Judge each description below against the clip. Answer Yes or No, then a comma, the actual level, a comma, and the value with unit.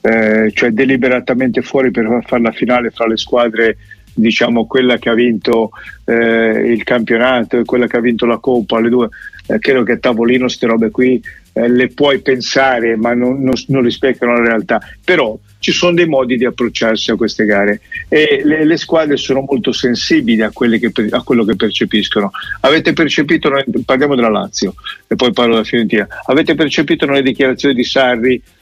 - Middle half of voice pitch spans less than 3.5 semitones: Yes, narrow, 2.6 semitones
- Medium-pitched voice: No, low, 120 Hz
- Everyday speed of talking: No, fast, 180 wpm